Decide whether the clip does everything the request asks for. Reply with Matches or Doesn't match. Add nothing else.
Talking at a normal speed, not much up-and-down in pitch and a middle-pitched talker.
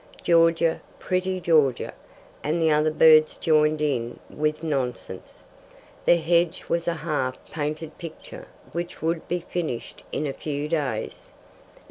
Doesn't match